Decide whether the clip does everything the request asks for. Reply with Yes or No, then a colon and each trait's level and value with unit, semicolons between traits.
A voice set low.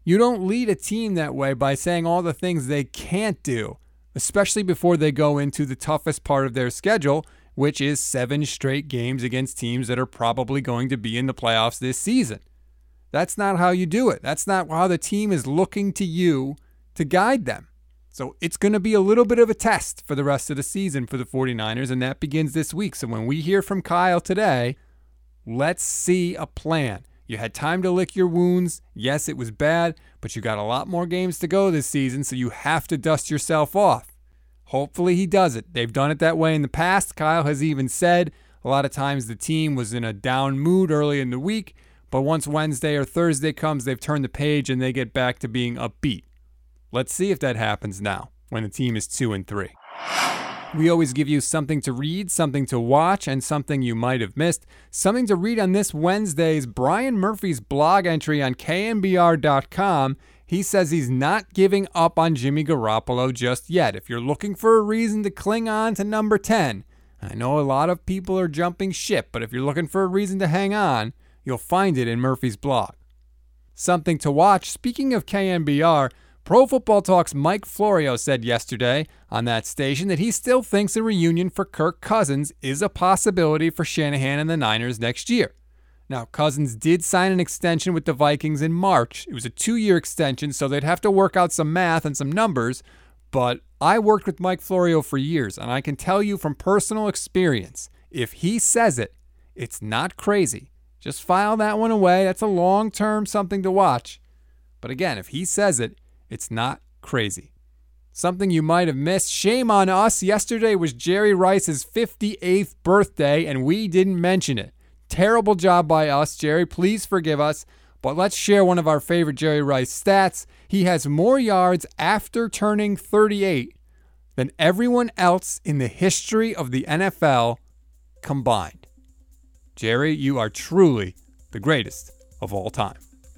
No: medium, 155 Hz